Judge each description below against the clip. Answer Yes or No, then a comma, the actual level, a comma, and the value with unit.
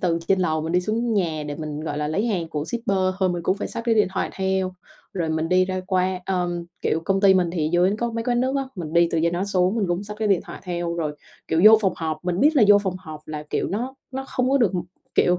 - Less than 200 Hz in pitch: Yes, medium, 185 Hz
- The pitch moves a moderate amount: Yes, average, 3.8 semitones